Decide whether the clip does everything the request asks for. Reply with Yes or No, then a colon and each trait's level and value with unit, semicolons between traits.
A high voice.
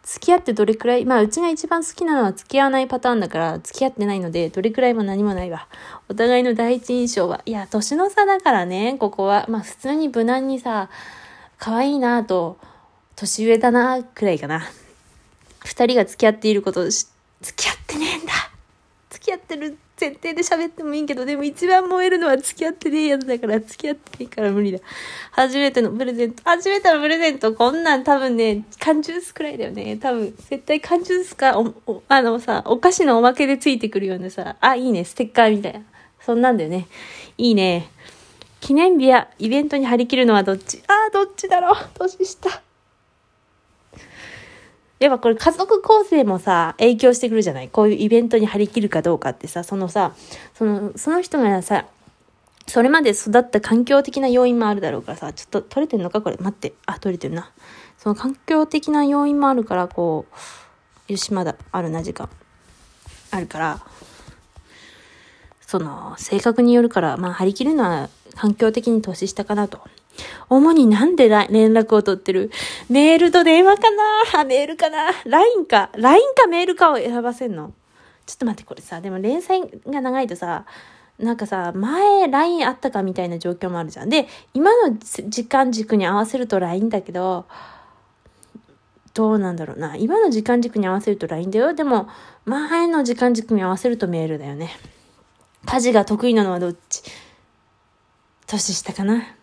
Yes: high, 240 Hz